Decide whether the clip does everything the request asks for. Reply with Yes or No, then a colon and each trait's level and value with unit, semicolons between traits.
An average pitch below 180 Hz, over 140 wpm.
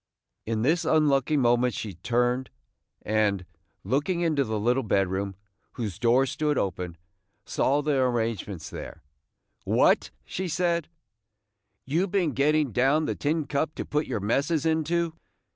No: low, 135 Hz; slow, 135 wpm